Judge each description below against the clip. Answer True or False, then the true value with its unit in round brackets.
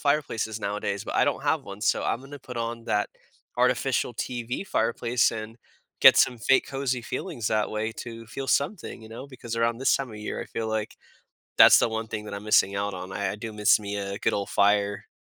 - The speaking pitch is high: False (115 Hz)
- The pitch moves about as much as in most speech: True (3.1 semitones)